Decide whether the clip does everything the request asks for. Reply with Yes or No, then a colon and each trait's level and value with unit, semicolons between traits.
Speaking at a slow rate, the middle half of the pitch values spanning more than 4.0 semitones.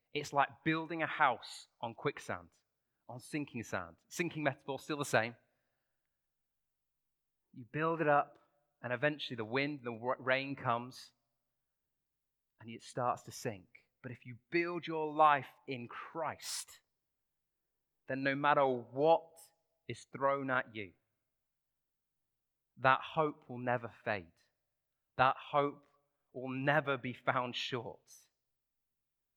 No: slow, 120 wpm; average, 3.2 semitones